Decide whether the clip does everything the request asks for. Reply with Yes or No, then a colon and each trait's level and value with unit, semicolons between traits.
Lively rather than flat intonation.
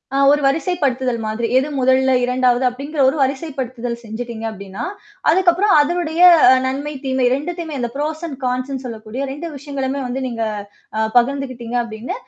No: average, 3.3 semitones